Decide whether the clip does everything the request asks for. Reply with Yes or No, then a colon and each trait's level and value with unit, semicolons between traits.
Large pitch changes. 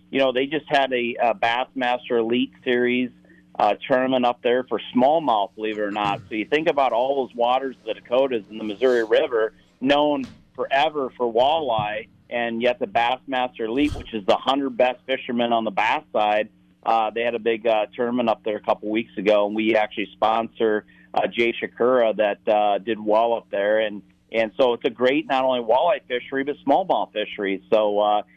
No: average, 3.0 semitones